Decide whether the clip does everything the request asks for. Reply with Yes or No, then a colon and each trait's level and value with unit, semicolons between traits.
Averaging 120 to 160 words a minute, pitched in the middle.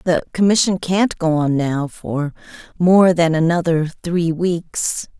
Yes: average, 140 wpm; medium, 170 Hz